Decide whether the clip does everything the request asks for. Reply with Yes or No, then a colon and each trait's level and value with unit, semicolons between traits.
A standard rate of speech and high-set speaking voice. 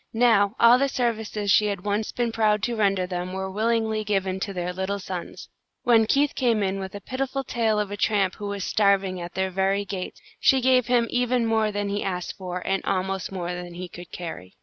No: fast, 215 wpm; high, 200 Hz